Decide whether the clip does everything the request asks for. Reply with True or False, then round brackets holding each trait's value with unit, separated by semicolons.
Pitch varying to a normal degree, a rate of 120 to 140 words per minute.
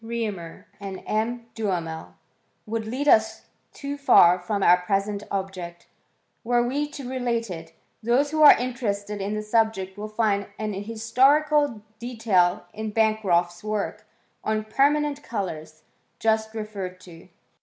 True (3.6 semitones; 135 wpm)